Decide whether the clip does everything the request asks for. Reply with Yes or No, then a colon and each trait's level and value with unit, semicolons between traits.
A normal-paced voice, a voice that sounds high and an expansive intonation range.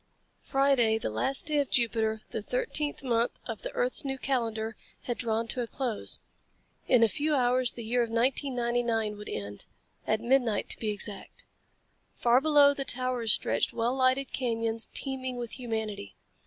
No: average, 165 wpm; high, 240 Hz; average, 3.1 semitones